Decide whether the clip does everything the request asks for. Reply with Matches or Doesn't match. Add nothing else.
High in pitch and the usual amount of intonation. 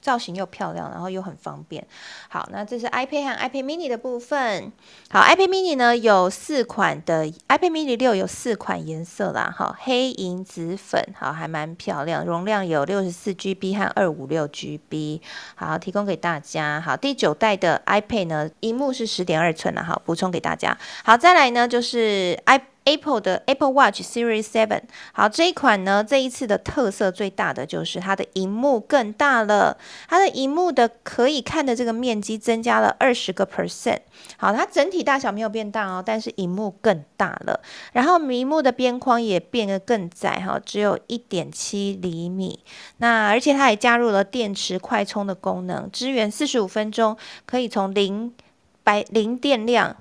Matches